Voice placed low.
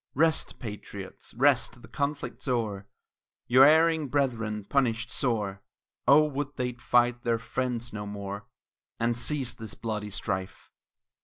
Yes: low, 120 Hz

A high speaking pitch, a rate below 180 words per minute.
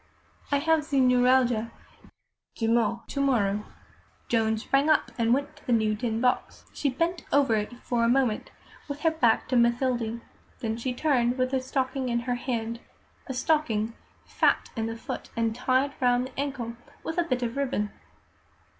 Yes: high, 245 Hz; average, 170 wpm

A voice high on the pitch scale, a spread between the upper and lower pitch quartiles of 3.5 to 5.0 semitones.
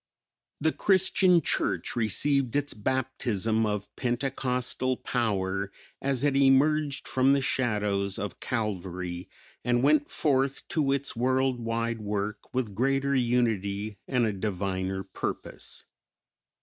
No: low, 120 Hz; average, 4.7 semitones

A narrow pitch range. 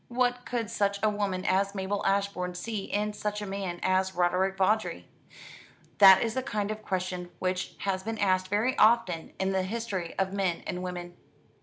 Yes: narrow, 2.1 semitones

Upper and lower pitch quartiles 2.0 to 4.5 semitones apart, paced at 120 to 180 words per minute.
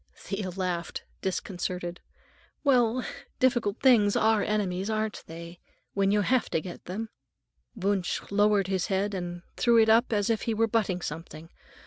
Yes: average, 3.5 semitones; average, 150 wpm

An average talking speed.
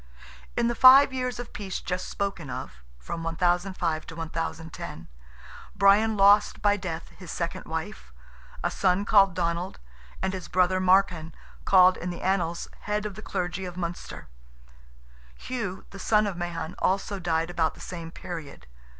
Yes: average, 155 wpm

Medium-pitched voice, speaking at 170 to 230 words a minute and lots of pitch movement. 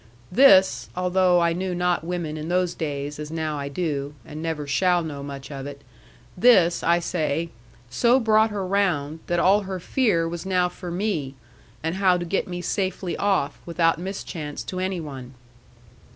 No: medium, 175 Hz; average, 175 wpm; average, 3.6 semitones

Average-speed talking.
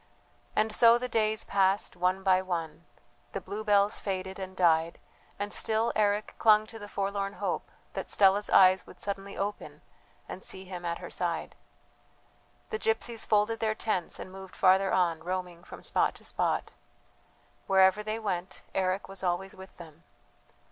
Yes: average, 160 wpm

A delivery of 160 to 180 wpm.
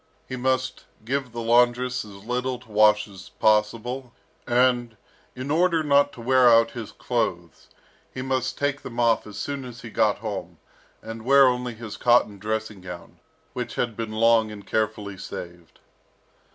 Yes: average, 165 wpm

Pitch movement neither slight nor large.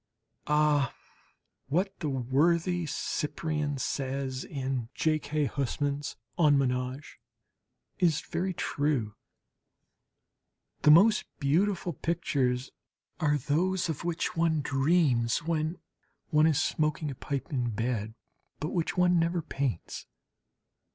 Yes: average, 3.6 semitones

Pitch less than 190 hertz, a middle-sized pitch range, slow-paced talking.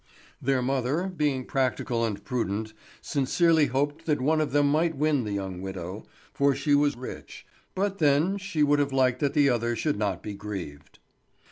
No: low, 135 Hz; average, 4.9 semitones; average, 175 wpm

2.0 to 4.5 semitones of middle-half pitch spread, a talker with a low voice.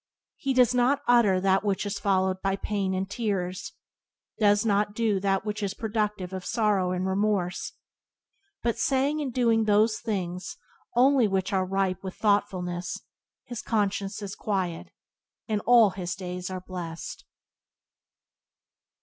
No: average, 2.8 semitones; high, 200 Hz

